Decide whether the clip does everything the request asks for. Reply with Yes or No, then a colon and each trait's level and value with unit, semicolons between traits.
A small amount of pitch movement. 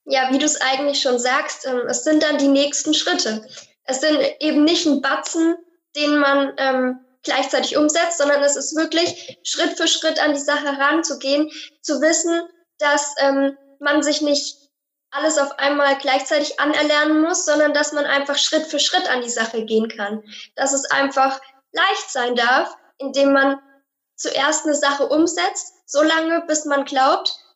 Yes: narrow, 1.9 semitones